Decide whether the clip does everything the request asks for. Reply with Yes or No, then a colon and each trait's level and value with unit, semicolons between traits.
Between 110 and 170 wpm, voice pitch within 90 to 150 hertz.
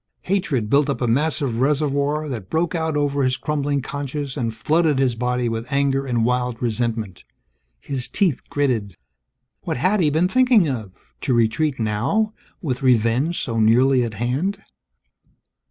Yes: average, 155 wpm; low, 135 Hz